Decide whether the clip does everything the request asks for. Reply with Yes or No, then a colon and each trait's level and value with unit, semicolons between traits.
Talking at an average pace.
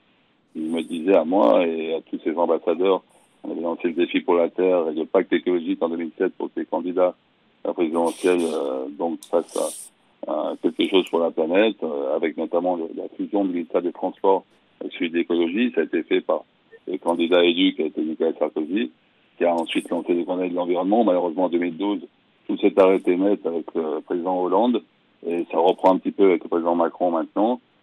Yes: average, 205 wpm